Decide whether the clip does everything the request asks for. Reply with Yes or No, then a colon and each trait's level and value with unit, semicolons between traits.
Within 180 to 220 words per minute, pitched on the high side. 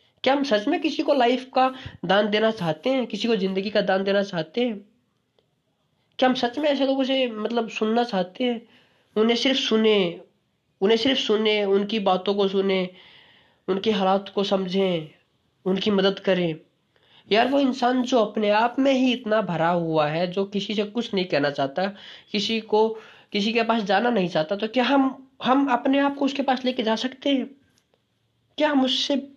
Yes: average, 185 wpm; high, 220 Hz